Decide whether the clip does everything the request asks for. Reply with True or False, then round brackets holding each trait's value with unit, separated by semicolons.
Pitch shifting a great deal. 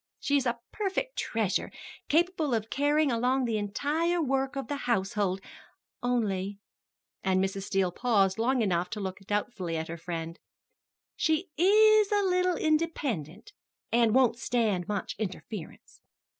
True (7.6 semitones)